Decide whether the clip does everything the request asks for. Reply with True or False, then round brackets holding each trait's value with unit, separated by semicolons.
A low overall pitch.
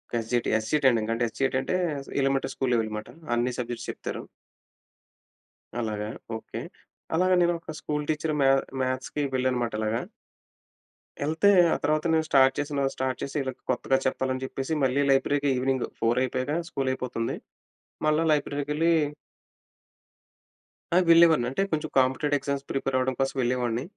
True (130 Hz)